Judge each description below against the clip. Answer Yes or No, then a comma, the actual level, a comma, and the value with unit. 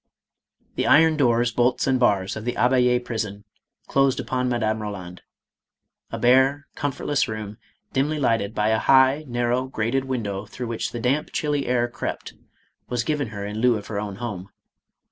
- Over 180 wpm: No, average, 165 wpm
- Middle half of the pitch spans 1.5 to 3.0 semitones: No, average, 3.5 semitones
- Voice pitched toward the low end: Yes, low, 120 Hz